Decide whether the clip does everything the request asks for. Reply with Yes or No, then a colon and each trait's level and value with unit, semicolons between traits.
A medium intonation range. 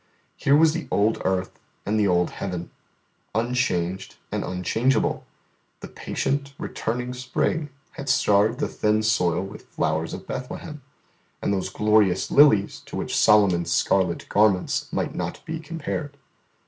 No: wide, 6.0 semitones